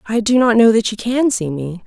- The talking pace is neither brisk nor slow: No, fast, 290 wpm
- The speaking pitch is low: No, high, 220 Hz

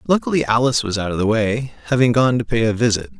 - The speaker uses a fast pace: Yes, fast, 245 wpm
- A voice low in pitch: Yes, low, 115 Hz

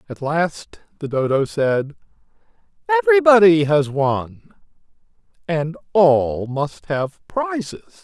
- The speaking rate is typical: No, slow, 95 wpm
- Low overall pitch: No, medium, 160 Hz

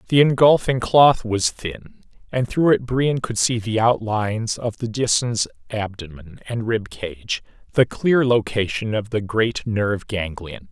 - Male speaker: Yes, male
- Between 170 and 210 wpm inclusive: No, average, 155 wpm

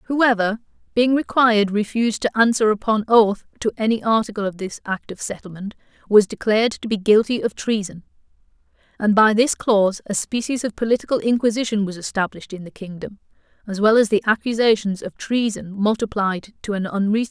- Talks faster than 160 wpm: Yes, average, 170 wpm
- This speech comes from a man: No, female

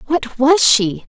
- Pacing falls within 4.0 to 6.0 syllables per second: No, 3.4 syllables/s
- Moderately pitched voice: No, very high, 265 Hz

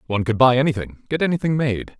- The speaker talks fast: Yes, fast, 210 wpm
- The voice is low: Yes, low, 130 Hz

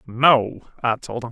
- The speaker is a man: Yes, male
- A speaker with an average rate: Yes, average, 180 wpm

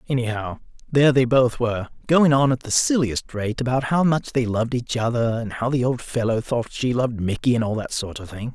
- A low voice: Yes, low, 120 Hz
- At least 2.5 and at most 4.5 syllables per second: No, 5.6 syllables/s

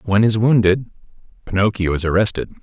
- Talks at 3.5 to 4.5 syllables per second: No, 6.1 syllables/s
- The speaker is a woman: No, male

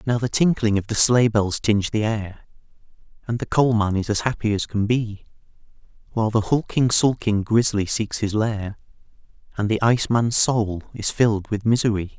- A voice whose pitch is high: No, low, 110 Hz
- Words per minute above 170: Yes, average, 180 wpm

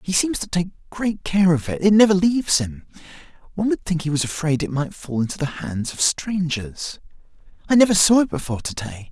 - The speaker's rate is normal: No, fast, 210 wpm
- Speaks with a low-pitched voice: No, medium, 165 Hz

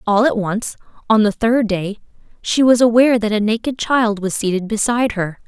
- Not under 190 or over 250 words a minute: Yes, average, 195 wpm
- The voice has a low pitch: No, high, 220 Hz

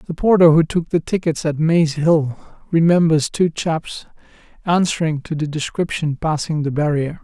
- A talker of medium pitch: Yes, medium, 160 Hz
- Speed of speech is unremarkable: Yes, average, 160 wpm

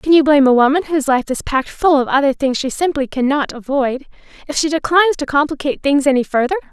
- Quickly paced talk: Yes, fast, 225 wpm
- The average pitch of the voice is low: No, very high, 285 Hz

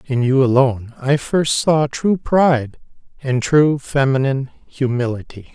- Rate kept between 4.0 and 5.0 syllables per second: Yes, 4.4 syllables/s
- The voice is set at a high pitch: No, low, 135 Hz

